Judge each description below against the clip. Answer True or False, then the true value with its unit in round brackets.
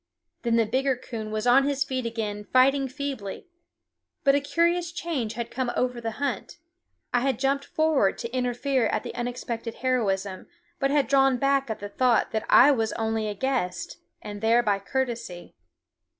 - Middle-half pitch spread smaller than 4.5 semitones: True (3.6 semitones)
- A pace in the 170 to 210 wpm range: True (175 wpm)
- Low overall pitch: False (250 Hz)